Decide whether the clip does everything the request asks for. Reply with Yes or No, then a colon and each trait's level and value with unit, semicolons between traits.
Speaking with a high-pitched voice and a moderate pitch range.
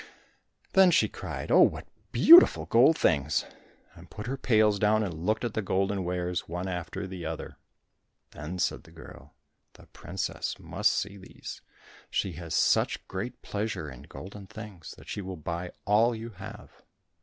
No: very low, 95 Hz; average, 3.8 semitones